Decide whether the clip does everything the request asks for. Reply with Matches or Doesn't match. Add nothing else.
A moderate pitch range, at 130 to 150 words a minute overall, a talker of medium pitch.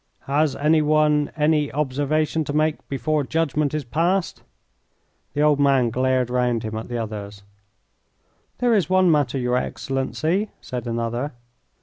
Matches